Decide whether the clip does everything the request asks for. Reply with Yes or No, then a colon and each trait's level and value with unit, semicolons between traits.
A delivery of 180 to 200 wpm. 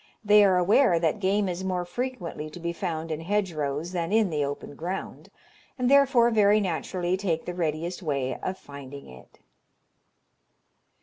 No: average, 160 wpm